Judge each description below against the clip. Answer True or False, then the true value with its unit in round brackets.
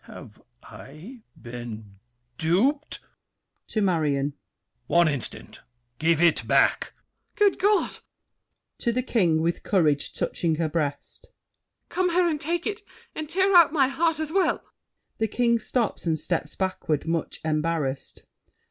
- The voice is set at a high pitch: False (180 Hz)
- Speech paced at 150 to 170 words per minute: False (135 wpm)